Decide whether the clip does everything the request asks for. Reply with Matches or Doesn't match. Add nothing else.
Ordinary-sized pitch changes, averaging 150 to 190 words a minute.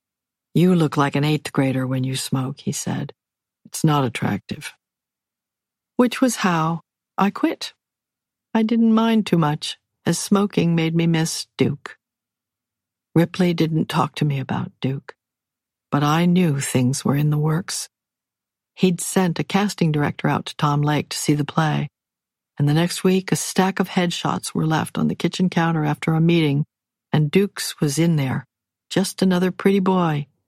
Matches